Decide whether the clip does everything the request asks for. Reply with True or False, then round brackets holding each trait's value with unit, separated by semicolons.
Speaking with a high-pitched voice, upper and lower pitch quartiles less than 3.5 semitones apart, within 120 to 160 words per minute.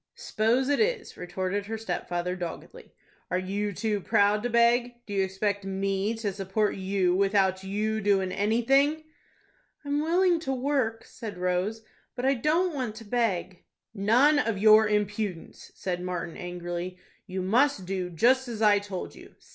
False (210 Hz; 4.1 semitones; 155 wpm)